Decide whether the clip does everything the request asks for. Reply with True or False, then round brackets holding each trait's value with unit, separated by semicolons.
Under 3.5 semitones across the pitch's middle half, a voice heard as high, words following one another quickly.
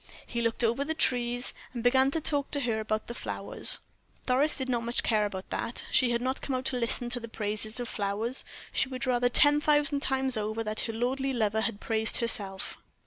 True (3.0 semitones; 240 Hz; 215 wpm)